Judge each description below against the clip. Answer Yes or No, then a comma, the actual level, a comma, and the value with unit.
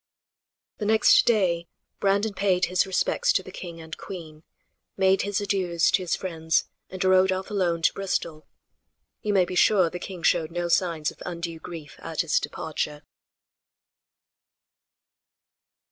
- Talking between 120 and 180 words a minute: Yes, average, 145 wpm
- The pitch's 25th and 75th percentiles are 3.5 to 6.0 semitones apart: No, average, 2.7 semitones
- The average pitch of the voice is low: No, medium, 180 Hz